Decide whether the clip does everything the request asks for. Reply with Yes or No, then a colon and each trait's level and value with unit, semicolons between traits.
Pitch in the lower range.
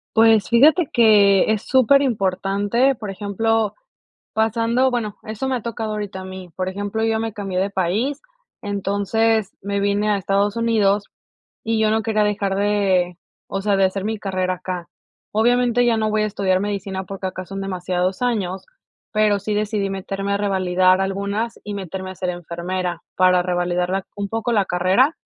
No: high, 200 Hz